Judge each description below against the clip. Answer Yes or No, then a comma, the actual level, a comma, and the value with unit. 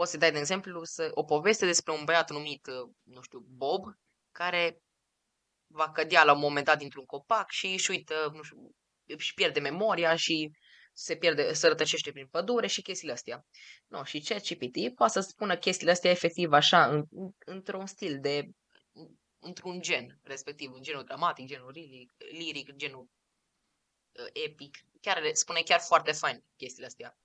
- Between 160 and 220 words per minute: Yes, average, 165 wpm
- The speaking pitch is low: No, medium, 165 Hz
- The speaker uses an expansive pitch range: No, average, 4.5 semitones